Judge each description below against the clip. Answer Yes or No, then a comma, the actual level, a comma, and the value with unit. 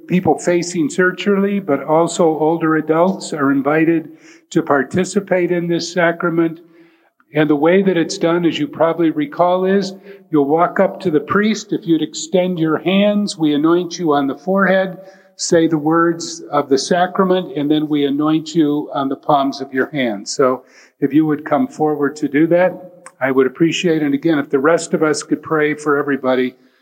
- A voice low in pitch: No, medium, 165 Hz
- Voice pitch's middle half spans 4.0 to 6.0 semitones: No, average, 3.3 semitones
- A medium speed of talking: Yes, average, 185 wpm